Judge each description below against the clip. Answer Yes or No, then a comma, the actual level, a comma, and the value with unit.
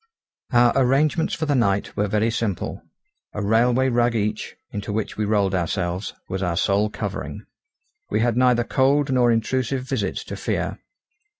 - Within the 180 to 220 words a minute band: No, average, 160 wpm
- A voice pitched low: Yes, low, 115 Hz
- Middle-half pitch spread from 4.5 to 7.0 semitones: No, average, 3.8 semitones